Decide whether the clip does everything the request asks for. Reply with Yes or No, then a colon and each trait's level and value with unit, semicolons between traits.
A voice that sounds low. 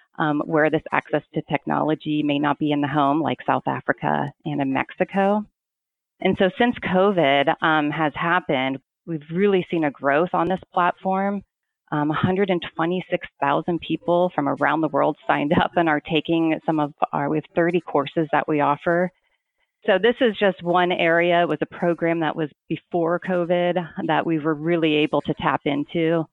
No: medium, 165 Hz